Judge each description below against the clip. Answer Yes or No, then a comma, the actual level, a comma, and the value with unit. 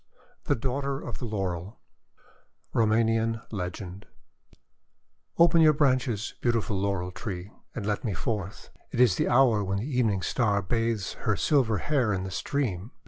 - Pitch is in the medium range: No, low, 110 Hz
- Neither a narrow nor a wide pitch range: Yes, average, 4.1 semitones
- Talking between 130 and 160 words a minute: Yes, average, 150 wpm